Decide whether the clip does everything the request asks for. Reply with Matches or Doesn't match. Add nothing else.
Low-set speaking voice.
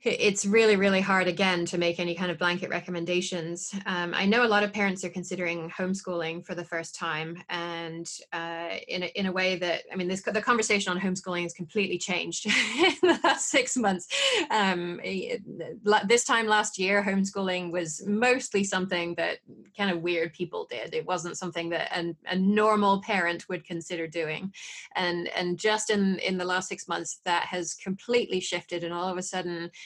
Doesn't match